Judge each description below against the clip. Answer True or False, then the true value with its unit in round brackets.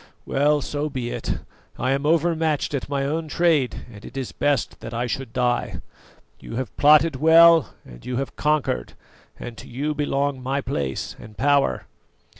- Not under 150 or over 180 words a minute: True (170 wpm)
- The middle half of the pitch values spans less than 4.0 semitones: True (3.4 semitones)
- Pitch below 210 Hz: True (140 Hz)